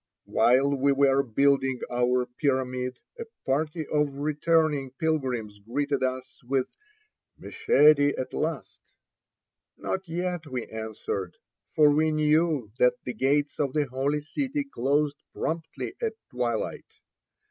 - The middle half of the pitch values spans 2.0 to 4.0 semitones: Yes, average, 3.2 semitones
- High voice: No, medium, 140 Hz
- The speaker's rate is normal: No, slow, 120 wpm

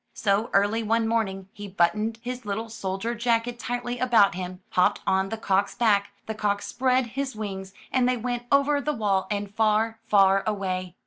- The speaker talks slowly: No, average, 180 wpm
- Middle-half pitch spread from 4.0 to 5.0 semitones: No, average, 3.3 semitones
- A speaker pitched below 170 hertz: No, high, 215 Hz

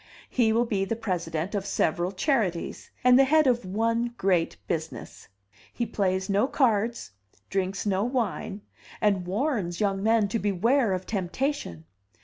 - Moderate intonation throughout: Yes, average, 4.0 semitones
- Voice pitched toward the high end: Yes, high, 205 Hz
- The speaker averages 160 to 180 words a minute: No, average, 145 wpm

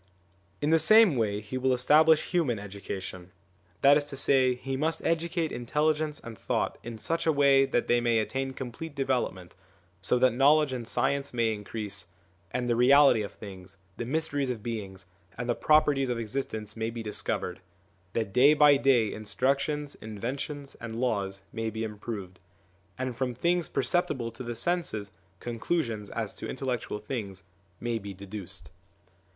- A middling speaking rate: Yes, average, 165 wpm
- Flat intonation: No, average, 4.6 semitones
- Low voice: Yes, low, 125 Hz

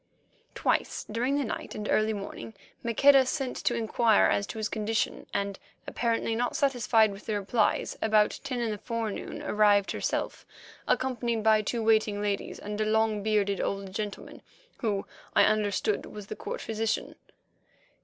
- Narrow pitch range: Yes, narrow, 2.0 semitones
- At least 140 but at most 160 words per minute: Yes, average, 155 wpm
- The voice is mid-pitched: No, high, 215 Hz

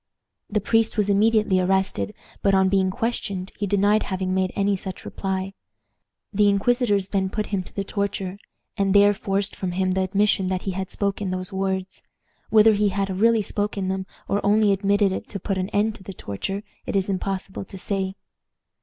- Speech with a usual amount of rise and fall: No, narrow, 1.4 semitones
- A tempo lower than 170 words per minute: No, average, 190 wpm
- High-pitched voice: Yes, high, 195 Hz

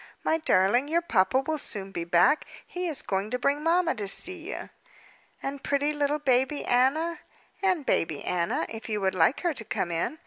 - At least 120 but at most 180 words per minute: No, average, 195 wpm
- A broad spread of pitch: Yes, wide, 8.0 semitones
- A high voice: Yes, very high, 275 Hz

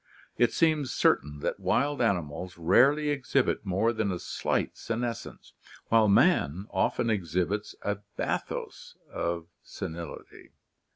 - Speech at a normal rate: No, slow, 115 wpm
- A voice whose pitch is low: Yes, low, 105 Hz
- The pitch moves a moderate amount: No, wide, 5.7 semitones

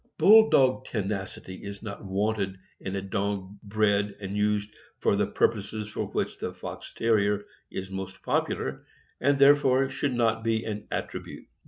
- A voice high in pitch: No, low, 105 Hz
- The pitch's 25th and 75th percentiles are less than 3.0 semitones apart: Yes, narrow, 2.4 semitones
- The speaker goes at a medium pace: Yes, average, 165 wpm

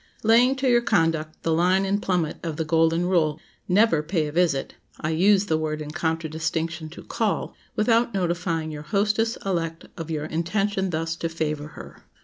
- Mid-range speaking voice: Yes, medium, 165 Hz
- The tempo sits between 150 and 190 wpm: Yes, average, 175 wpm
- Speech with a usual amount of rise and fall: Yes, average, 3.6 semitones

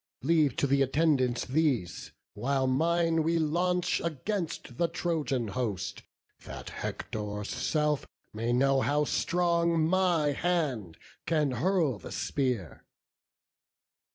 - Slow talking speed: Yes, slow, 110 wpm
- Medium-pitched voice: Yes, medium, 150 Hz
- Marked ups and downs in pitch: No, average, 4.9 semitones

